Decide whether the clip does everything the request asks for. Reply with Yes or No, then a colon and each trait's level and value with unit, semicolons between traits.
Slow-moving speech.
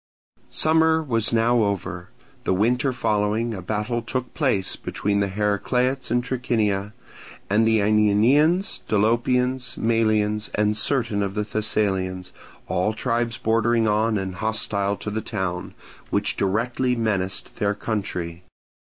Yes: slow, 125 wpm